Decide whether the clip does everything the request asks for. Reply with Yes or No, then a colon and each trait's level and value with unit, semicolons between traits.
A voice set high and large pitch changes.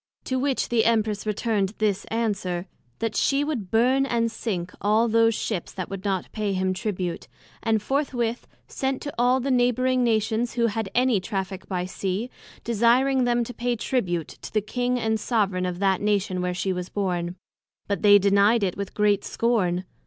No: high, 215 Hz; average, 3.8 semitones